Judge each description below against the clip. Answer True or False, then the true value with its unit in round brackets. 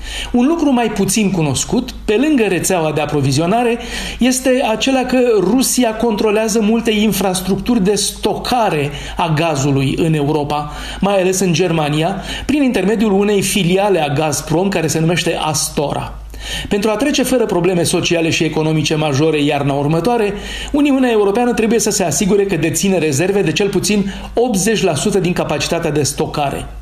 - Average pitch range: False (5.8 semitones)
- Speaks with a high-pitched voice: True (195 Hz)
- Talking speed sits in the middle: True (145 wpm)